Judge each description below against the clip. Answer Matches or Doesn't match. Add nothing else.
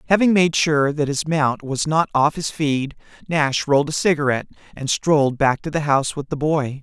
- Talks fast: Matches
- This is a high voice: Doesn't match